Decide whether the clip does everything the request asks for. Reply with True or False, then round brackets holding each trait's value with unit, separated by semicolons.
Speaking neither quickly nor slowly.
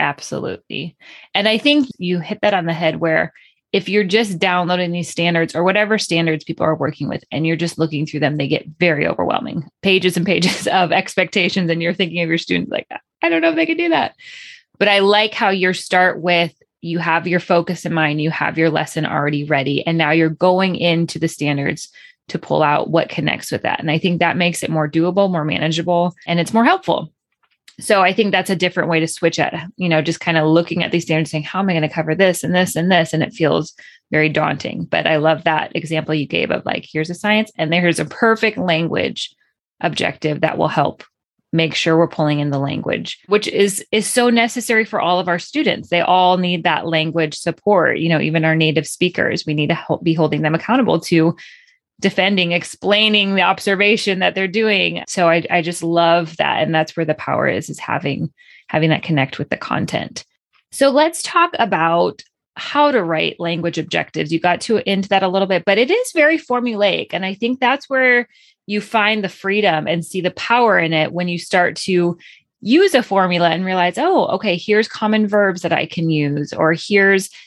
False (220 wpm)